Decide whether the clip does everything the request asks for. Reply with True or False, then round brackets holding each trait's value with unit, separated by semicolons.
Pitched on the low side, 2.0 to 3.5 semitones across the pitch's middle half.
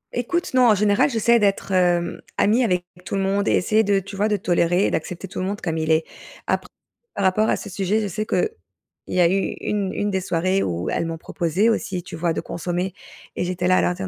False (190 Hz; 2.8 semitones)